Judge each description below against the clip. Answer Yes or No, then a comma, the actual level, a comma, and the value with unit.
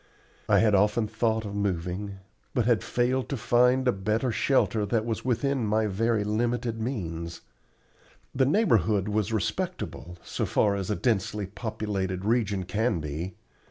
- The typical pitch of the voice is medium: No, low, 110 Hz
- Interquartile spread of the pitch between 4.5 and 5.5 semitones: No, average, 3.3 semitones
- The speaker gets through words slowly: No, average, 150 wpm